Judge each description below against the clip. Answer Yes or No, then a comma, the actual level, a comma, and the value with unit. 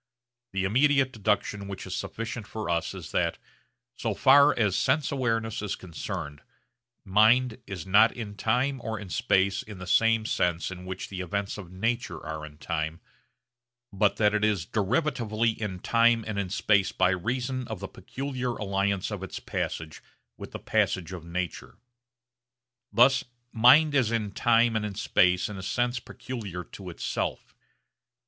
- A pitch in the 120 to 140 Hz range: No, low, 105 Hz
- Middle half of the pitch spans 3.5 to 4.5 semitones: Yes, average, 4.0 semitones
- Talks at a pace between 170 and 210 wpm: No, average, 160 wpm